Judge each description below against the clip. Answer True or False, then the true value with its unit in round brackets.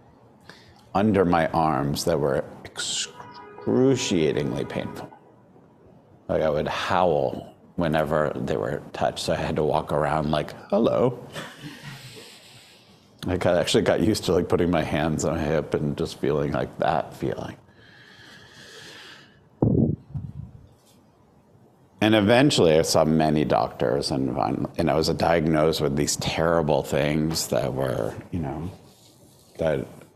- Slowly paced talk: True (120 wpm)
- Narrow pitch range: True (1.8 semitones)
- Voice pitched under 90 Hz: True (80 Hz)